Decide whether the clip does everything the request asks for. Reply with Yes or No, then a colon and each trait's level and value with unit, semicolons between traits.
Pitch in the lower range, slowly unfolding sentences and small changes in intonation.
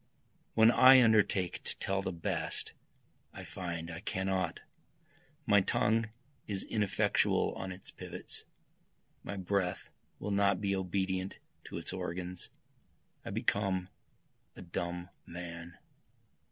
Yes: very low, 95 Hz; slow, 115 wpm; narrow, 2.3 semitones